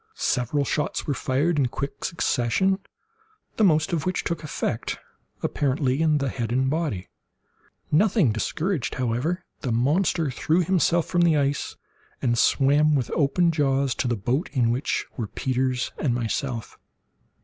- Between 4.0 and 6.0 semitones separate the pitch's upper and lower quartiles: Yes, average, 4.5 semitones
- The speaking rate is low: No, average, 150 wpm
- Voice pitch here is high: No, medium, 140 Hz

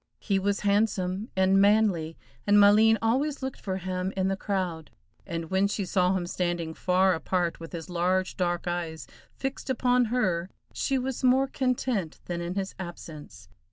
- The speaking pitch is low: No, high, 190 Hz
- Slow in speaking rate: No, average, 165 wpm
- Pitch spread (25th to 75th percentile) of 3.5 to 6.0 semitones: Yes, average, 3.8 semitones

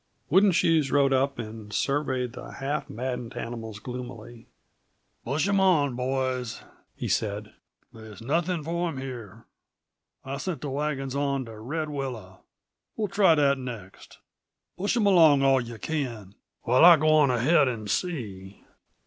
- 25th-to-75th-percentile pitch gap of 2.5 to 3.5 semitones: No, average, 4.8 semitones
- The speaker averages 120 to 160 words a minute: Yes, average, 150 wpm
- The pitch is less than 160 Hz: Yes, low, 135 Hz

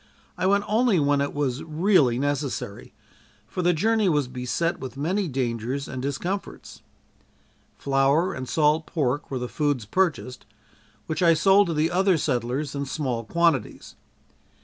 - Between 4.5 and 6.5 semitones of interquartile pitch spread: Yes, average, 4.8 semitones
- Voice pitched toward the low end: No, medium, 145 Hz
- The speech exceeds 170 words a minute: No, average, 150 wpm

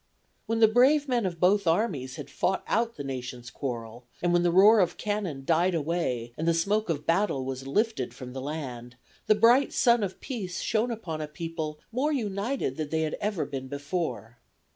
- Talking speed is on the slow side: No, average, 195 wpm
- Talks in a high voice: No, medium, 170 Hz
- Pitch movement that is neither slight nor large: No, wide, 7.6 semitones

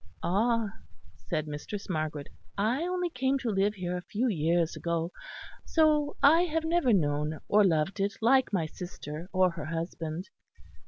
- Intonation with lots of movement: Yes, wide, 7.4 semitones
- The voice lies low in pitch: No, high, 195 Hz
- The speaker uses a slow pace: No, average, 155 wpm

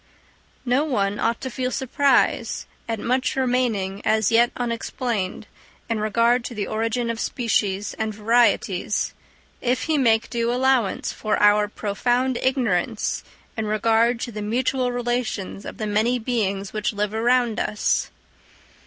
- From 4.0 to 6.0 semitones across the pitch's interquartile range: No, average, 2.8 semitones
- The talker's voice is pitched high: Yes, high, 230 Hz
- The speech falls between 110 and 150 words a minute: Yes, average, 140 wpm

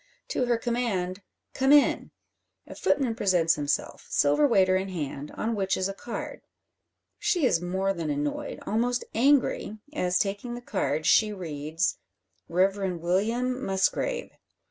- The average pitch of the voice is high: Yes, high, 195 Hz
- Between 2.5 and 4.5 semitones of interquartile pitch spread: No, wide, 5.4 semitones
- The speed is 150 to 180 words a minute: No, average, 140 wpm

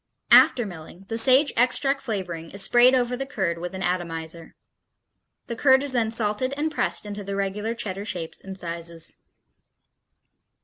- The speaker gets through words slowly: No, average, 160 wpm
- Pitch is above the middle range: Yes, high, 205 Hz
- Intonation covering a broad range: Yes, wide, 5.9 semitones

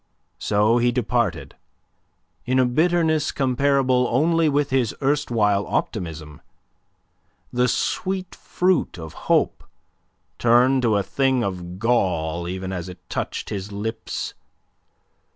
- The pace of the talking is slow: Yes, slow, 115 wpm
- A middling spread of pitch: No, wide, 6.0 semitones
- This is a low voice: Yes, low, 120 Hz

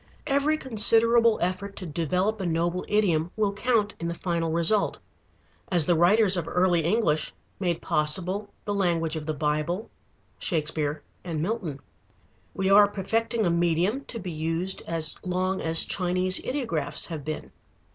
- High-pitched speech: No, medium, 180 Hz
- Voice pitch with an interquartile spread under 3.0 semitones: No, average, 4.0 semitones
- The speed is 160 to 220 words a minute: No, average, 150 wpm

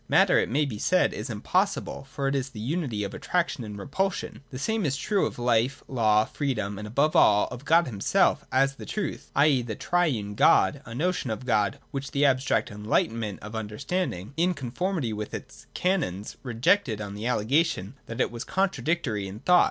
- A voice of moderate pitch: No, low, 130 Hz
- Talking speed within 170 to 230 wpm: Yes, average, 190 wpm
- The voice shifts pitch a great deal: Yes, wide, 6.7 semitones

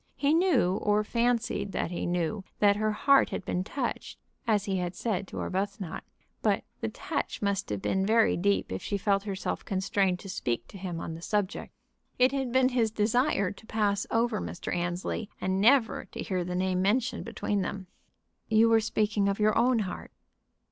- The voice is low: No, high, 205 Hz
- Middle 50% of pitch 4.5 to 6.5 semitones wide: No, average, 3.3 semitones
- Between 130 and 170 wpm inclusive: No, average, 190 wpm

